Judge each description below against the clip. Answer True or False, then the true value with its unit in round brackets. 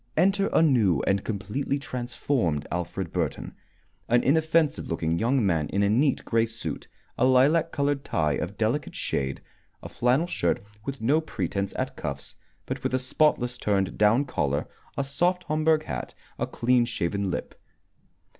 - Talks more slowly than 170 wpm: True (155 wpm)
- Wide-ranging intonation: True (6.5 semitones)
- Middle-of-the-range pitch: False (120 Hz)